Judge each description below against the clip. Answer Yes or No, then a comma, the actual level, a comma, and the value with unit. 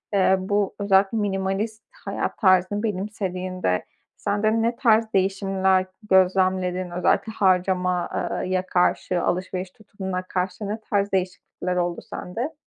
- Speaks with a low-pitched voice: No, high, 190 Hz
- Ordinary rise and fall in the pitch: No, narrow, 2.0 semitones